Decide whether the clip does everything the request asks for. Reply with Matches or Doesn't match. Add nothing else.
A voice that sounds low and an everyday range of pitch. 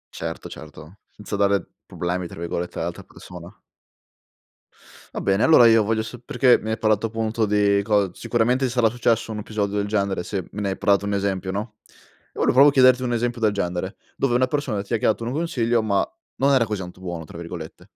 Matches